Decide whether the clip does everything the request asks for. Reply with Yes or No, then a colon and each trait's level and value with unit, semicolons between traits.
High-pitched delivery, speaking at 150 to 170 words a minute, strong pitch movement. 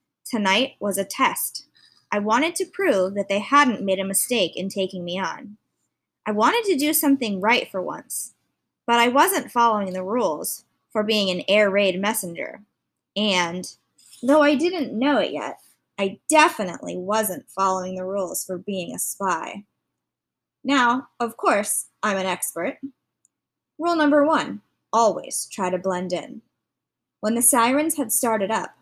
Yes: high, 215 Hz; average, 155 wpm; wide, 6.3 semitones